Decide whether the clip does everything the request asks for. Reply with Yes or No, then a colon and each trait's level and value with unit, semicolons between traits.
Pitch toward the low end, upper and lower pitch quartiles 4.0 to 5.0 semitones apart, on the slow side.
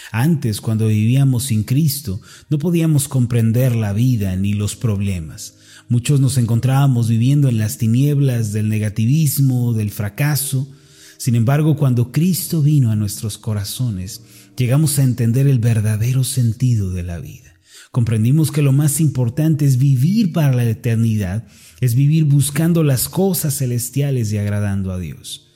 No: low, 125 Hz; average, 4.3 semitones; average, 145 wpm